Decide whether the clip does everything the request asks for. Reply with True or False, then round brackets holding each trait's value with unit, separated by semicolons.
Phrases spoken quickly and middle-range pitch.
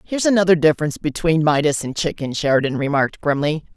False (160 wpm; 155 Hz)